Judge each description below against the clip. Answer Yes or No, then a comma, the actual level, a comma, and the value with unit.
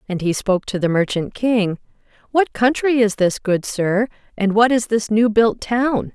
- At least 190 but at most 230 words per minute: Yes, average, 195 wpm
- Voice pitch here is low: No, high, 220 Hz